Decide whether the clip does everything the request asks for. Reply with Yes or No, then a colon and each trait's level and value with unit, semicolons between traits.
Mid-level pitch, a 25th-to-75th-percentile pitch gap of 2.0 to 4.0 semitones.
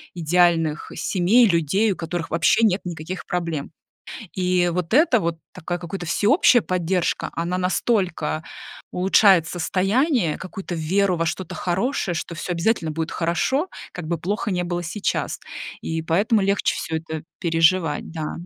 Yes: medium, 175 Hz; average, 2.8 semitones